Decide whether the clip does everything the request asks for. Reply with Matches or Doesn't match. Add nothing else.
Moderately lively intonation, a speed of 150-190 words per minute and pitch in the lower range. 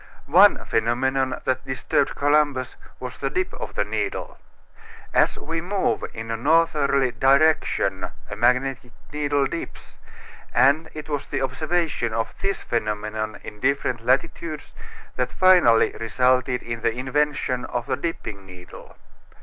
Doesn't match